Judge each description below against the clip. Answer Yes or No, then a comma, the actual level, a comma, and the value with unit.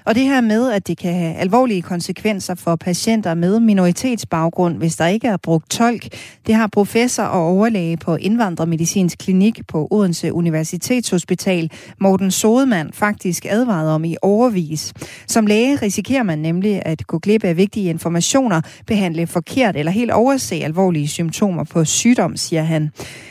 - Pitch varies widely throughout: No, average, 4.7 semitones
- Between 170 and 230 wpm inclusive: No, average, 155 wpm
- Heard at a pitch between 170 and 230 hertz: Yes, medium, 185 Hz